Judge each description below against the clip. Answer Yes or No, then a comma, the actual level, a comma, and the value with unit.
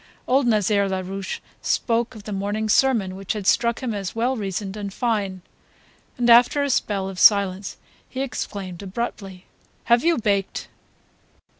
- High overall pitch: Yes, high, 205 Hz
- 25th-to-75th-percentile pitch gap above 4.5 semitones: No, average, 3.4 semitones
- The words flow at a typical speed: Yes, average, 150 wpm